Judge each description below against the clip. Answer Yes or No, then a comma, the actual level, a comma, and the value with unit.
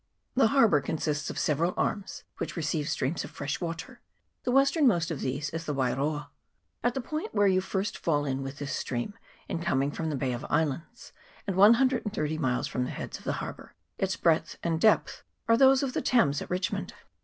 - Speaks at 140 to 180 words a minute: No, average, 200 wpm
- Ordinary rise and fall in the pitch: No, wide, 7.0 semitones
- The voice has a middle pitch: Yes, medium, 165 Hz